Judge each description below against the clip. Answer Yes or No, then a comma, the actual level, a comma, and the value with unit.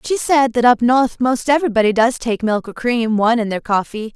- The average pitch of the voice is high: Yes, high, 235 Hz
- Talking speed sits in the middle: No, fast, 230 wpm